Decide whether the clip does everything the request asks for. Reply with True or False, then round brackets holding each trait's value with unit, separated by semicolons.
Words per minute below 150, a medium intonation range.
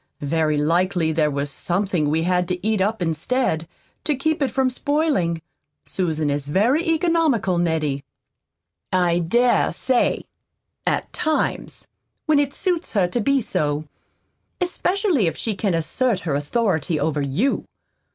False (140 wpm; 8.6 semitones)